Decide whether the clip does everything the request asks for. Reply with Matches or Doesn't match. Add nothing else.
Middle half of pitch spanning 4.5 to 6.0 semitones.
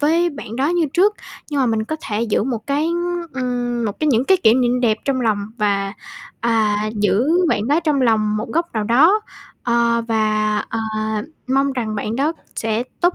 Matches